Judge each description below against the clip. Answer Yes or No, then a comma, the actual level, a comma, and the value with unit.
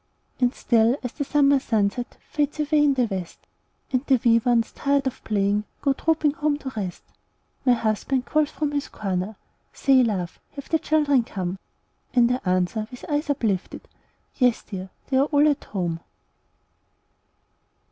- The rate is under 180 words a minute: Yes, average, 160 wpm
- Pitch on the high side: Yes, very high, 250 Hz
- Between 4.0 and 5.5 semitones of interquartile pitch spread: Yes, average, 5.2 semitones